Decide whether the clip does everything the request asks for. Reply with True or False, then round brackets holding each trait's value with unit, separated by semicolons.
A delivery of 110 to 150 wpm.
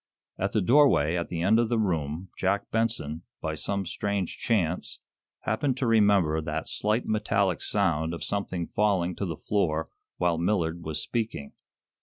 False (160 wpm)